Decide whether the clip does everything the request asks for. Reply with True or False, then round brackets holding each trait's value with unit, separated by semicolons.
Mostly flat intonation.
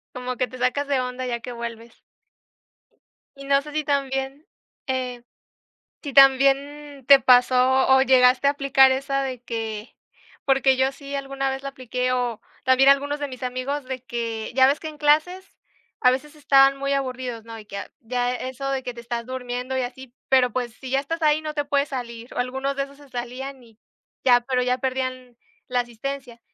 True (1.8 semitones)